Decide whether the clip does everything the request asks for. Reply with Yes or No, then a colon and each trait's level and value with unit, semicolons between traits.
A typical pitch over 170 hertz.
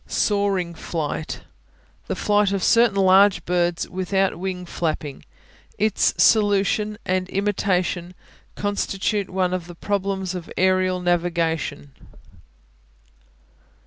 Yes: medium, 185 Hz